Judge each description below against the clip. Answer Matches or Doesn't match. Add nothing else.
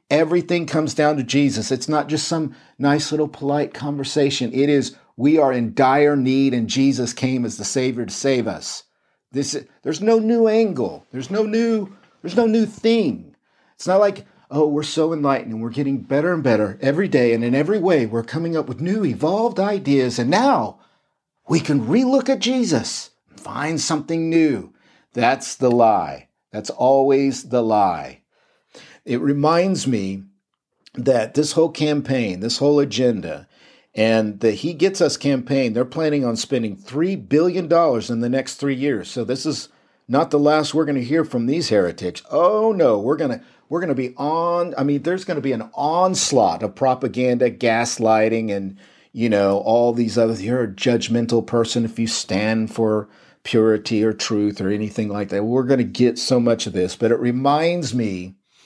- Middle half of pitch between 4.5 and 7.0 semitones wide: Matches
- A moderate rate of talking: Matches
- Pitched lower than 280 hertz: Matches